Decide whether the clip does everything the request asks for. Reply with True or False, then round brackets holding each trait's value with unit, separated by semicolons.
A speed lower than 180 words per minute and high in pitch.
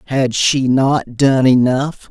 False (140 wpm; 130 Hz)